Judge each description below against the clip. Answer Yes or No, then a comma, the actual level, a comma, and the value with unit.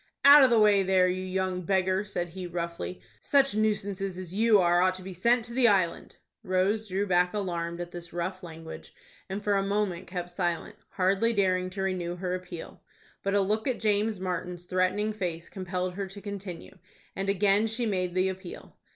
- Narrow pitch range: Yes, narrow, 2.2 semitones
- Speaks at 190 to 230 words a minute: Yes, average, 195 wpm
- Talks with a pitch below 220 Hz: Yes, medium, 185 Hz